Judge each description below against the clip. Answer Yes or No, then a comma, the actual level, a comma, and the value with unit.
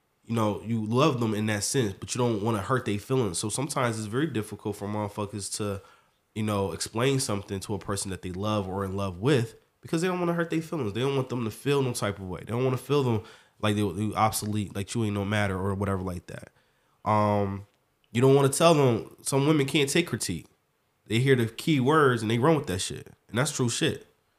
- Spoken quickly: Yes, fast, 250 wpm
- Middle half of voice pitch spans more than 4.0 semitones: Yes, average, 4.4 semitones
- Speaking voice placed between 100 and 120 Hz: Yes, low, 110 Hz